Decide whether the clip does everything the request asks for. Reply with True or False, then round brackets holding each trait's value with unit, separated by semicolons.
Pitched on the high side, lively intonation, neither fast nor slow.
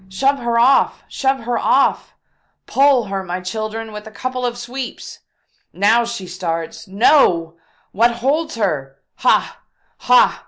False (225 Hz; 4.8 semitones; 155 wpm)